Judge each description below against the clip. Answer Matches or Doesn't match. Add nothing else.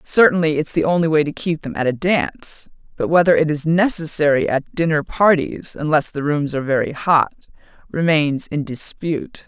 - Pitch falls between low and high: Matches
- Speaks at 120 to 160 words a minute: Doesn't match